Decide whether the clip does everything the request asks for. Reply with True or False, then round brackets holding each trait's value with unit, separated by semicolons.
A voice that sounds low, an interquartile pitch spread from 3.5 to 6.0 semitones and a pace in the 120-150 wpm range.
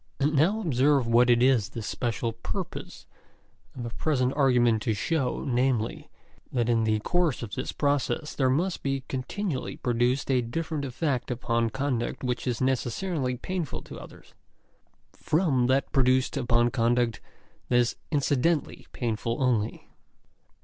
False (130 Hz; 3.0 semitones; 140 wpm)